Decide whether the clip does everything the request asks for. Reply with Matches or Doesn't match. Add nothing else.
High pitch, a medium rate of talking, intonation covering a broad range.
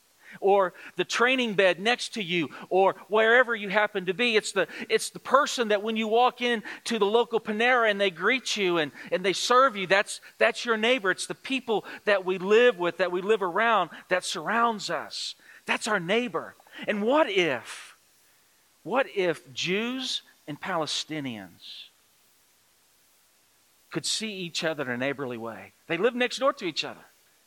Doesn't match